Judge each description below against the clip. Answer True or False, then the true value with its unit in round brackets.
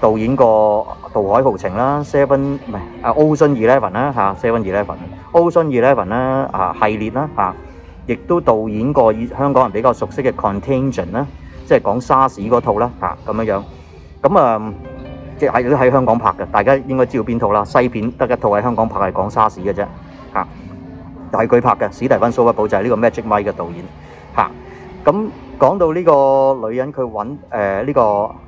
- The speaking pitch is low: True (115 Hz)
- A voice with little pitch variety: False (5.1 semitones)